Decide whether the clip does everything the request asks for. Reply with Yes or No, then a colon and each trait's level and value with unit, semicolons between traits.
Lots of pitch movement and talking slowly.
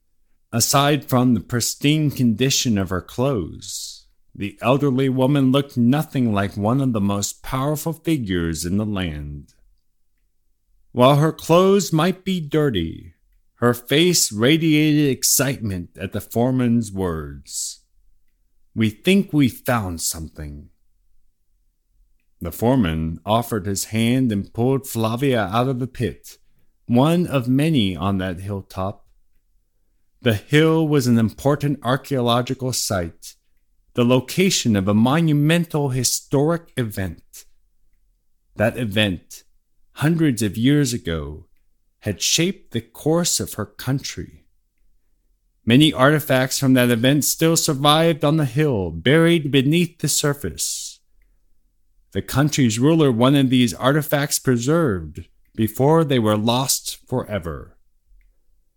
Yes: wide, 6.4 semitones; slow, 115 wpm